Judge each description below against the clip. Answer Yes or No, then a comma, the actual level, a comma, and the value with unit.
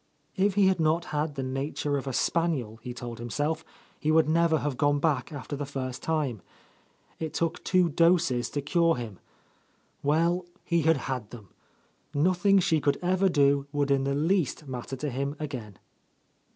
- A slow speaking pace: No, average, 175 wpm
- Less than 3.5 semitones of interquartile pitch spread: No, average, 3.8 semitones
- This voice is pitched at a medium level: Yes, medium, 145 Hz